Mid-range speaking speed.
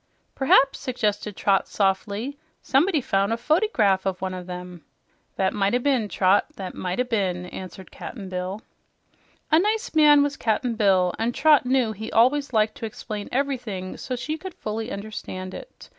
Yes: average, 170 wpm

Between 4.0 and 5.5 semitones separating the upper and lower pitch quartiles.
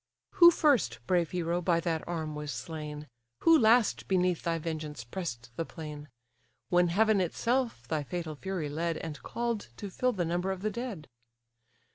Yes: average, 4.5 semitones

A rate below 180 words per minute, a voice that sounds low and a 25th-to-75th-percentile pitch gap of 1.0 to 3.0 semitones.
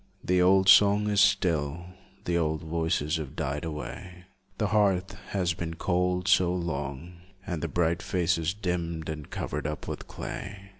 Yes: average, 155 wpm; very low, 85 Hz; narrow, 2.5 semitones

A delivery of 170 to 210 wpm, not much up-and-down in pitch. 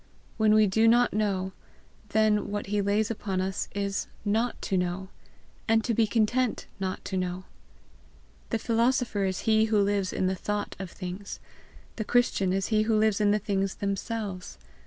Yes: average, 175 wpm; narrow, 2.3 semitones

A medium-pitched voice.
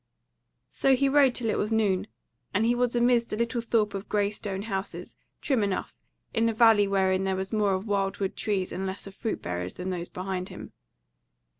No: high, 205 Hz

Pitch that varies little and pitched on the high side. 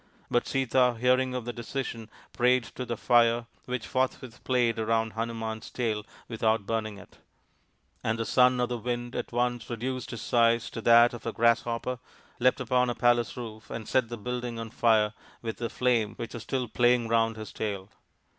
No: narrow, 1.7 semitones; low, 120 Hz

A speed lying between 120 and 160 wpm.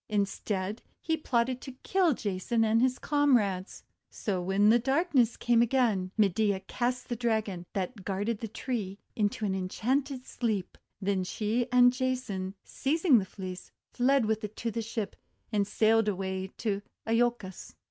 Yes: average, 150 wpm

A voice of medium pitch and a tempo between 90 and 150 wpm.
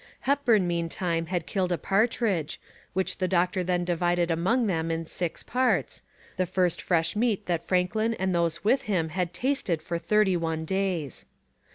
No: medium, 180 Hz; average, 165 wpm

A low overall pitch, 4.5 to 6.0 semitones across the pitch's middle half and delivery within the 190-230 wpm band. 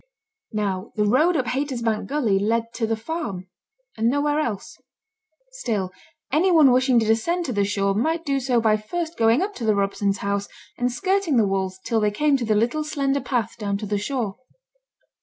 No: high, 230 Hz; wide, 5.6 semitones; average, 195 wpm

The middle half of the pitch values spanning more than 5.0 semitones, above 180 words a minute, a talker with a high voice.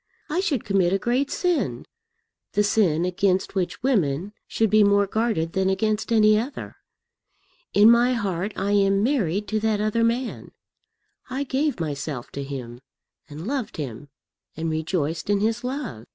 No: wide, 5.5 semitones; average, 155 wpm; high, 205 Hz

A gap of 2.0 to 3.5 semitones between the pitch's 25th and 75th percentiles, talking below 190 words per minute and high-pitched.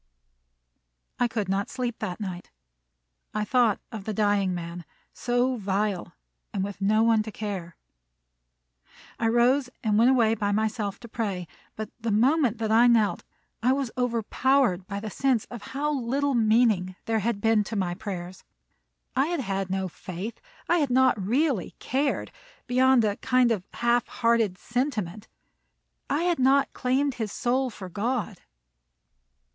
No: average, 3.9 semitones; average, 155 wpm; high, 225 Hz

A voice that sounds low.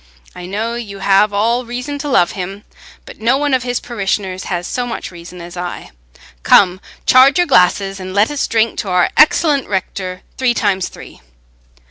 No: high, 205 Hz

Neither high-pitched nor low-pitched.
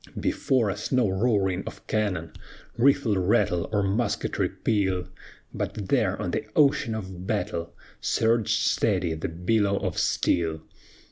No: low, 100 Hz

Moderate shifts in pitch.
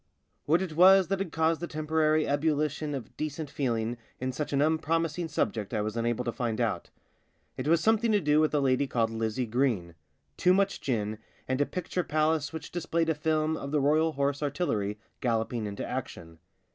Yes: average, 4.8 semitones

